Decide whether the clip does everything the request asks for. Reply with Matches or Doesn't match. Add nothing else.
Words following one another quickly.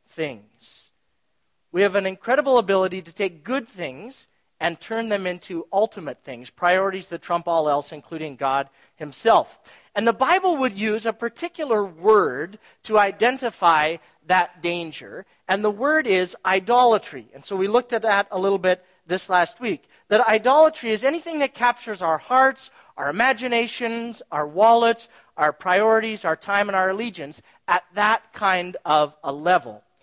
Doesn't match